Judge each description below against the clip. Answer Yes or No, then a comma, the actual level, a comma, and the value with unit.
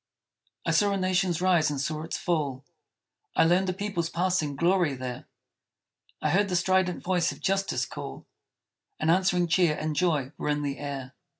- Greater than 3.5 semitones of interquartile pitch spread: Yes, average, 3.9 semitones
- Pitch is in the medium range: Yes, medium, 170 Hz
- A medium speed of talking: Yes, average, 175 wpm